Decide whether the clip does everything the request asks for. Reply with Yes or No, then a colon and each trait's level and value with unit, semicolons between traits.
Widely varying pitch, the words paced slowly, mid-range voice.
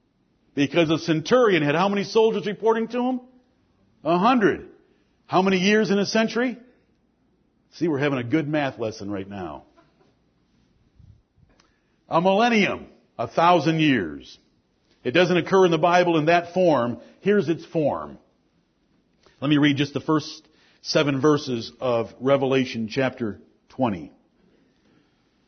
Yes: wide, 6.5 semitones; slow, 130 wpm; medium, 165 Hz